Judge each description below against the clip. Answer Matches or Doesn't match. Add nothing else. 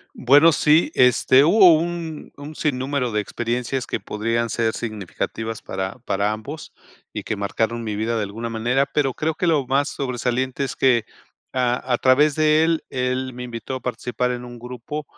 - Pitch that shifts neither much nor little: Matches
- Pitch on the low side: Matches